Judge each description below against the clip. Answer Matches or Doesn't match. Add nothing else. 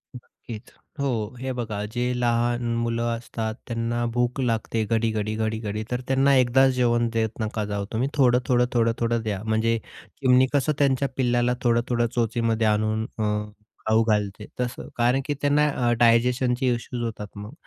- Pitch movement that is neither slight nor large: Doesn't match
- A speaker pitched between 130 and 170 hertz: Doesn't match